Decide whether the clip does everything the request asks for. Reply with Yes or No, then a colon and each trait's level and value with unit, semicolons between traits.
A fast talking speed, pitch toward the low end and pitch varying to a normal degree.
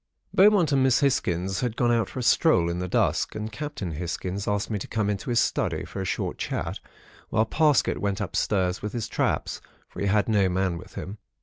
Yes: fast, 215 wpm; low, 105 Hz; average, 4.3 semitones